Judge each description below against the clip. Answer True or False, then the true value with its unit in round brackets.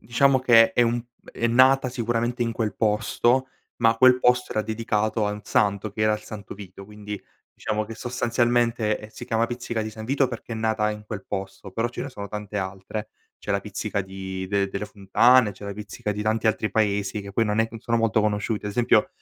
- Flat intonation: True (2.3 semitones)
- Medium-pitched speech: False (110 Hz)